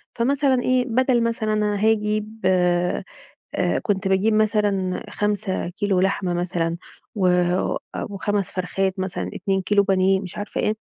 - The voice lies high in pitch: Yes, high, 200 Hz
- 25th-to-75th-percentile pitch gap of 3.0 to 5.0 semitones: No, narrow, 2.5 semitones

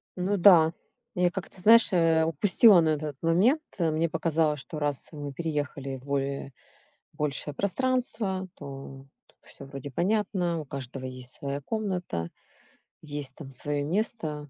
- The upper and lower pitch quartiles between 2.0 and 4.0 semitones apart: No, average, 4.6 semitones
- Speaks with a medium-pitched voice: Yes, medium, 155 Hz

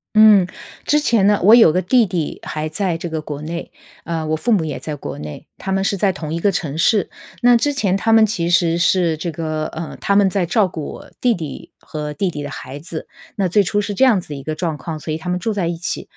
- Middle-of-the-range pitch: Yes, medium, 175 Hz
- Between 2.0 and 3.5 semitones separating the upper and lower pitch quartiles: No, average, 4.5 semitones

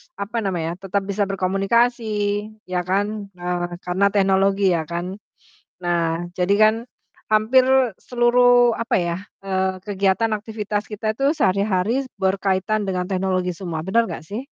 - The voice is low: No, high, 195 Hz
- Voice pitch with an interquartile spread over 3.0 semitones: No, average, 2.7 semitones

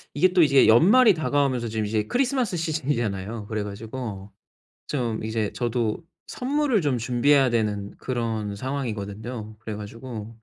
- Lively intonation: No, average, 5.0 semitones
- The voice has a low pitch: Yes, low, 120 Hz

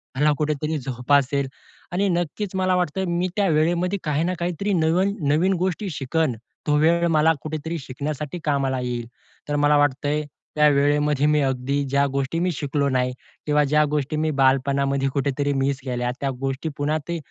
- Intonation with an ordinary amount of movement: Yes, average, 3.1 semitones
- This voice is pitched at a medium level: Yes, medium, 150 Hz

